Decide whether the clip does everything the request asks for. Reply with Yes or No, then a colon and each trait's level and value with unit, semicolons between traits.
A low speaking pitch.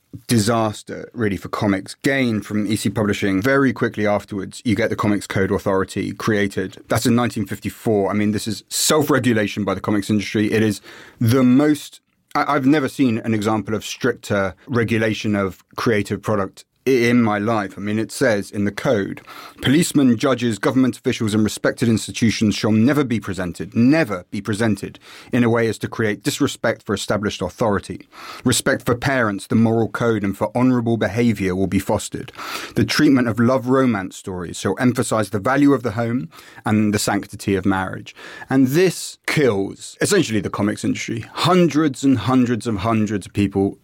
Yes: low, 110 Hz